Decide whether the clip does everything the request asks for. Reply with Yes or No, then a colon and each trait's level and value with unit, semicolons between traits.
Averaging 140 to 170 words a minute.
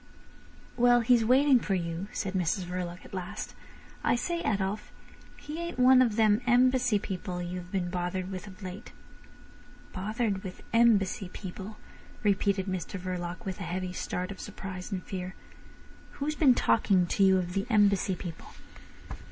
Yes: average, 155 wpm